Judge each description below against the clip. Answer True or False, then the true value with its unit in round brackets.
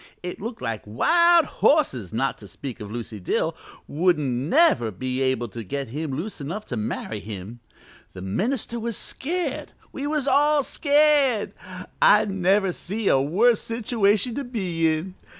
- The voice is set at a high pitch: False (180 Hz)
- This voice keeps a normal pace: True (155 wpm)